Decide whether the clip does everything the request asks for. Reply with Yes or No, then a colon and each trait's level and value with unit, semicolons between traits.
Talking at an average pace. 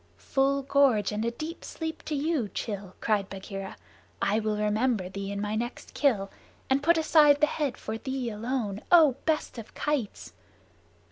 Yes: average, 165 wpm